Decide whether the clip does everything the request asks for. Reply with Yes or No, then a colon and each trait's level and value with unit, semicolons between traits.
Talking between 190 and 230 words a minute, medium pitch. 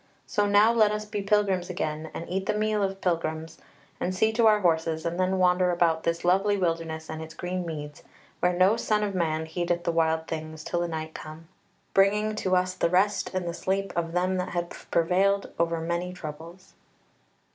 Yes: average, 200 wpm; medium, 180 Hz